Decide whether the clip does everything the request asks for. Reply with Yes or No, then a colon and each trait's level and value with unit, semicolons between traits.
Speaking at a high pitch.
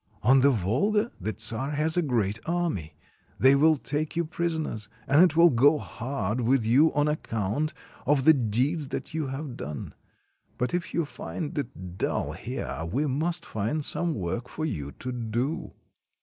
No: medium, 140 Hz